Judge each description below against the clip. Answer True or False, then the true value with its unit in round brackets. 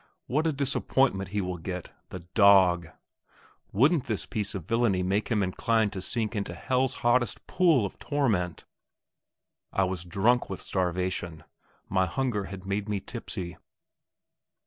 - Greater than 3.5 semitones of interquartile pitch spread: True (4.5 semitones)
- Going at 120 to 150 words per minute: True (145 wpm)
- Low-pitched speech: True (100 Hz)